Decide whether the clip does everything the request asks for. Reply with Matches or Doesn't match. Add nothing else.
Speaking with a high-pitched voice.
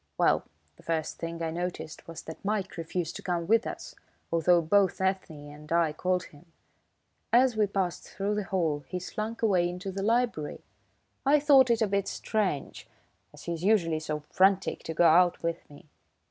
Doesn't match